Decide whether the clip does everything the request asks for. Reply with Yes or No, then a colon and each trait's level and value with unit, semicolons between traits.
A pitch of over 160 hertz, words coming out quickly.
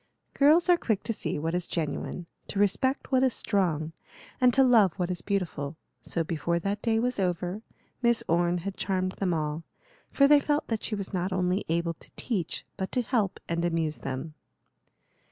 No: medium, 185 Hz; average, 190 wpm